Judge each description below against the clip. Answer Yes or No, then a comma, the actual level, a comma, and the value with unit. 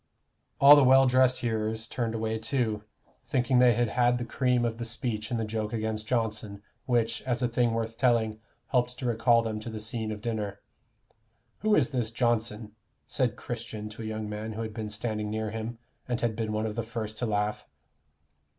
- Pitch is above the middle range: No, low, 115 Hz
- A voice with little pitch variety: Yes, narrow, 1.9 semitones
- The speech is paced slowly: No, average, 200 wpm